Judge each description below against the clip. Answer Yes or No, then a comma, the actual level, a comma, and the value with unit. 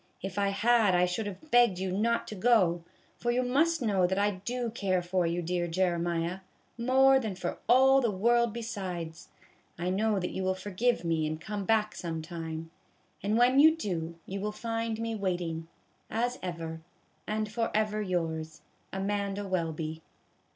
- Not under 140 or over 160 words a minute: No, average, 170 wpm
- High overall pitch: Yes, high, 195 Hz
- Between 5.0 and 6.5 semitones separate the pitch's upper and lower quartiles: No, average, 4.6 semitones